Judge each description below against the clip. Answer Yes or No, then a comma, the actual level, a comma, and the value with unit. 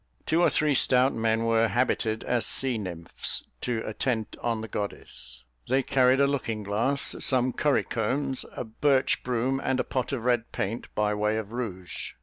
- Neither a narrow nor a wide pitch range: Yes, average, 3.2 semitones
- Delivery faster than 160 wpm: Yes, average, 175 wpm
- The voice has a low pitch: Yes, low, 120 Hz